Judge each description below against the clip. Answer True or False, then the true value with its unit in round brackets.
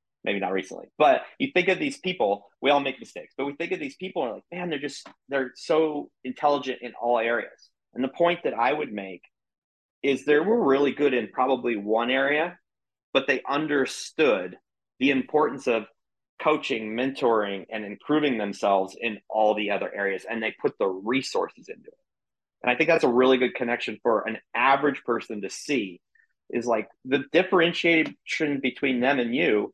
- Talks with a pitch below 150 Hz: True (135 Hz)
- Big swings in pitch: False (5.0 semitones)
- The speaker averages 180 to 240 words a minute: True (185 wpm)